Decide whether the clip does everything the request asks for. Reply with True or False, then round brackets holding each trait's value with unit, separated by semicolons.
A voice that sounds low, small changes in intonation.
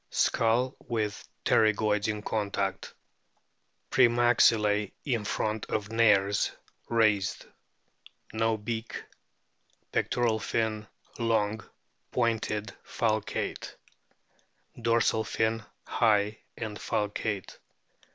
True (110 Hz; 1.6 semitones)